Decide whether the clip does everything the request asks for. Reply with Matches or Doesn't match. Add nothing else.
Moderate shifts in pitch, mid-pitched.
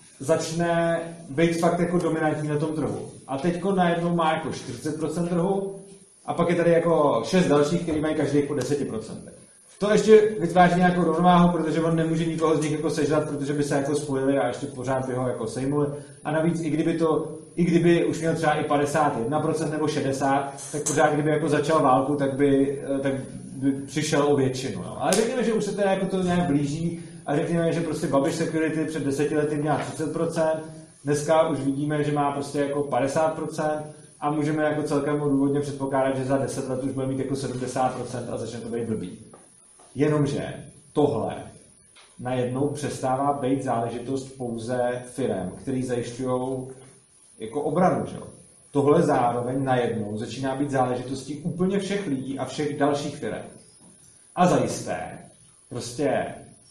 Matches